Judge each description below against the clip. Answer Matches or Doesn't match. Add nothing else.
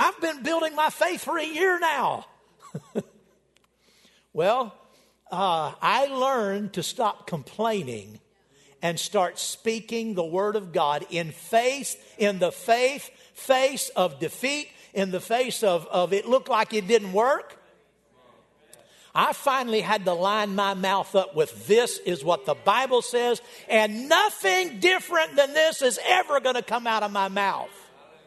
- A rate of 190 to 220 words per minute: Doesn't match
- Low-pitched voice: Doesn't match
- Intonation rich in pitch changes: Matches